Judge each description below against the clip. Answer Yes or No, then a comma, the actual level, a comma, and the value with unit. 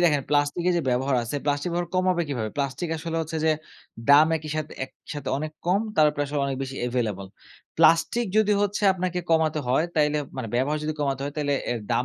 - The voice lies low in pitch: No, medium, 150 Hz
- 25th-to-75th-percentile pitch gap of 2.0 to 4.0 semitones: Yes, average, 3.3 semitones